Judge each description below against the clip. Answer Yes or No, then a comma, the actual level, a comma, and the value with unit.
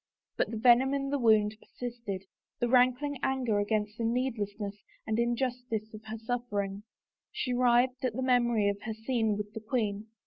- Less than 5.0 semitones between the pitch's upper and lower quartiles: Yes, average, 2.9 semitones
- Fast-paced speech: No, average, 175 wpm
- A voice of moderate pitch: No, high, 230 Hz